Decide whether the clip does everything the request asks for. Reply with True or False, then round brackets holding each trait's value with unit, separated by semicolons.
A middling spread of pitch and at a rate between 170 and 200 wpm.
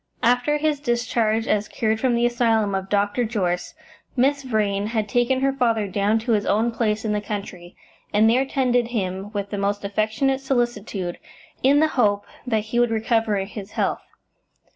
True (3.0 semitones; 175 wpm)